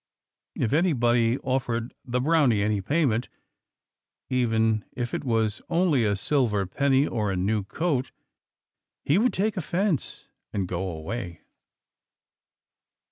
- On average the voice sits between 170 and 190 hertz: No, low, 120 Hz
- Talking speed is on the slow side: Yes, slow, 120 wpm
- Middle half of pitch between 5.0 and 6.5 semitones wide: Yes, wide, 5.4 semitones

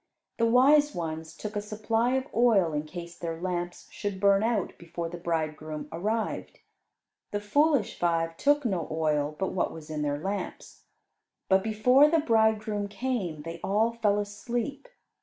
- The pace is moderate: Yes, average, 160 wpm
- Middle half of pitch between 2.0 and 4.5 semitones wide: No, wide, 5.5 semitones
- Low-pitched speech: No, high, 200 Hz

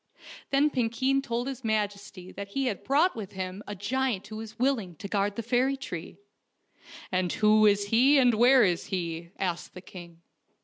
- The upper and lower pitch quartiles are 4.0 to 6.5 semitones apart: Yes, average, 5.1 semitones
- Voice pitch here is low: No, high, 215 Hz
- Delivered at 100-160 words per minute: No, average, 185 wpm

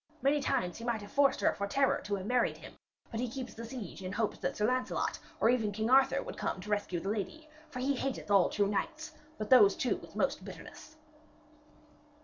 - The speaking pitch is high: Yes, high, 230 Hz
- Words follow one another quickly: Yes, fast, 220 wpm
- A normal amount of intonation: Yes, average, 4.6 semitones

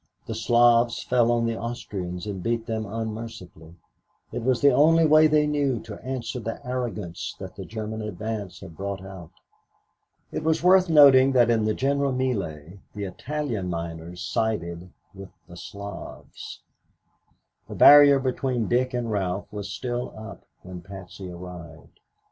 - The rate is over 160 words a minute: No, average, 150 wpm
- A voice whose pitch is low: Yes, low, 110 Hz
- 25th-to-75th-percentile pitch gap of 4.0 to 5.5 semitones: Yes, average, 5.1 semitones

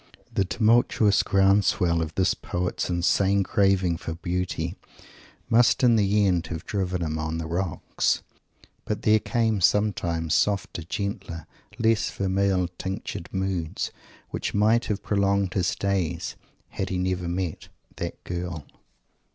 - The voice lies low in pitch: Yes, very low, 95 Hz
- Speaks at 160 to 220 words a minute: No, slow, 135 wpm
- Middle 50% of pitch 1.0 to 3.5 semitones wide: Yes, narrow, 2.6 semitones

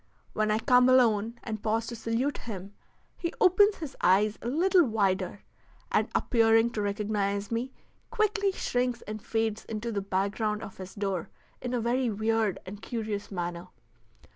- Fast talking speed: No, average, 160 wpm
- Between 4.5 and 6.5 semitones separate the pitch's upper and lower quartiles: No, average, 3.3 semitones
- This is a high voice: Yes, high, 220 Hz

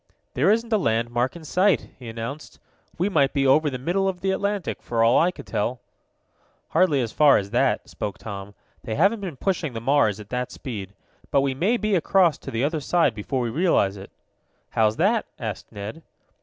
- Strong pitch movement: Yes, wide, 8.0 semitones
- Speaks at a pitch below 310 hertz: Yes, medium, 140 Hz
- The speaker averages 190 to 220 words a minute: Yes, average, 200 wpm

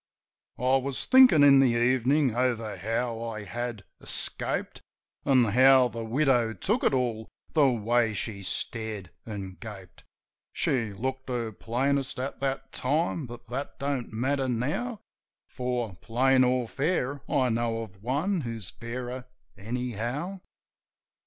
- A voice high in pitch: No, low, 125 Hz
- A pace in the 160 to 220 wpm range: No, slow, 135 wpm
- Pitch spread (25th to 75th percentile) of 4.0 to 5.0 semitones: No, average, 3.0 semitones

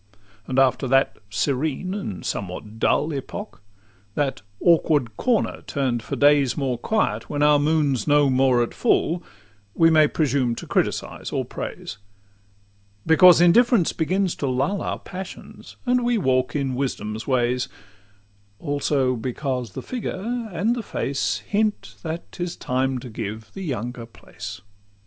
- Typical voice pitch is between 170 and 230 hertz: No, medium, 140 Hz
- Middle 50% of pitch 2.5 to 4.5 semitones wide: No, wide, 5.4 semitones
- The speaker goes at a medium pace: Yes, average, 145 wpm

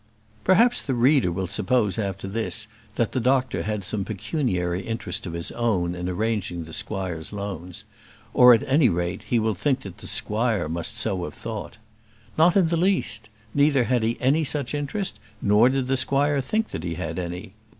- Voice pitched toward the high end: No, low, 110 Hz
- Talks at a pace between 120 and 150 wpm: No, average, 185 wpm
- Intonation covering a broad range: Yes, wide, 6.4 semitones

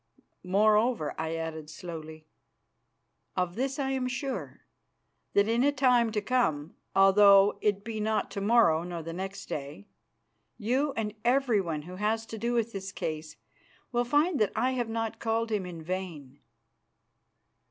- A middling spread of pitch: No, wide, 5.7 semitones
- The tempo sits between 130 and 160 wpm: Yes, average, 155 wpm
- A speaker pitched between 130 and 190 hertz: No, high, 210 Hz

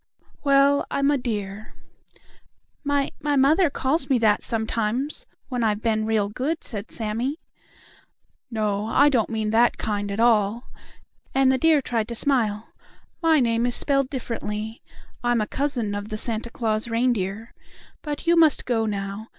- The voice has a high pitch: Yes, high, 235 Hz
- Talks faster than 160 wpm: No, average, 155 wpm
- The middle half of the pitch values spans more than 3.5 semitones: Yes, average, 4.3 semitones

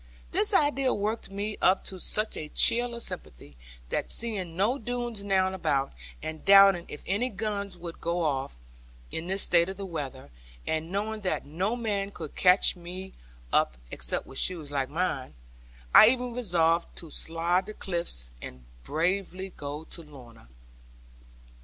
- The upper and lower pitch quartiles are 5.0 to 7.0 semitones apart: No, average, 4.3 semitones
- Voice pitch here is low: No, medium, 185 Hz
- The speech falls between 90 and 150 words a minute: No, average, 160 wpm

